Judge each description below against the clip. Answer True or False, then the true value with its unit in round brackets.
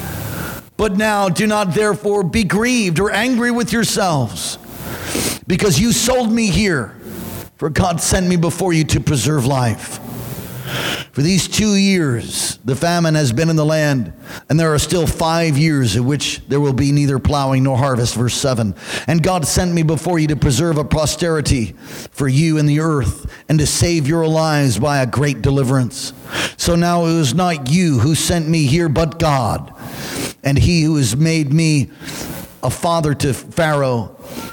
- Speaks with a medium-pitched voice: True (155 Hz)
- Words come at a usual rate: True (170 wpm)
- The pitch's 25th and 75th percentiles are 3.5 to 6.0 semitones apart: True (4.2 semitones)